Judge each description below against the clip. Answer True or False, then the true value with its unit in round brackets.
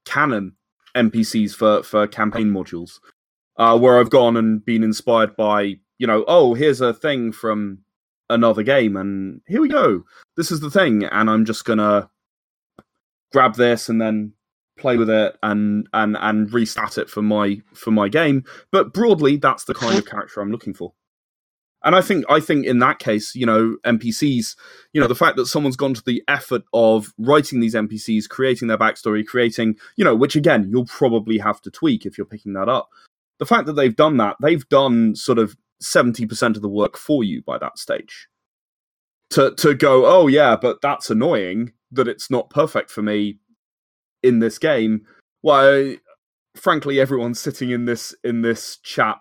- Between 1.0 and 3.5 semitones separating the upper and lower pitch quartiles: True (2.9 semitones)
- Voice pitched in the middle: False (115 Hz)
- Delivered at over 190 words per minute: False (185 wpm)